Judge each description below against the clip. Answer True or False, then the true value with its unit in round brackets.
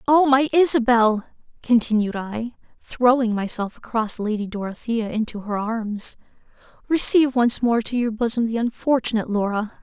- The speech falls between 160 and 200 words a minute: False (135 wpm)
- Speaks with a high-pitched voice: True (230 Hz)